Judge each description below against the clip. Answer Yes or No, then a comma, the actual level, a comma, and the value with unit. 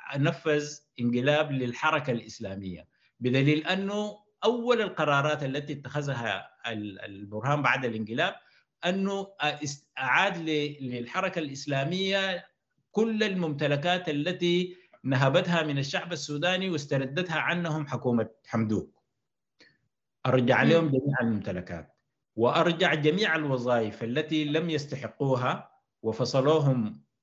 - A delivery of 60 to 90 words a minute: Yes, average, 85 wpm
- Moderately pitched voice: Yes, medium, 150 Hz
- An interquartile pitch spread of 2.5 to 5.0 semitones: No, wide, 5.4 semitones